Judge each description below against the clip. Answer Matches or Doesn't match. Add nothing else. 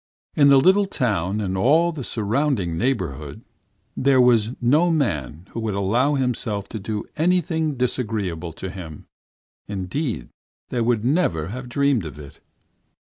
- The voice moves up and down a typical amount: Doesn't match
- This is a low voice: Matches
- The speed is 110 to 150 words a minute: Matches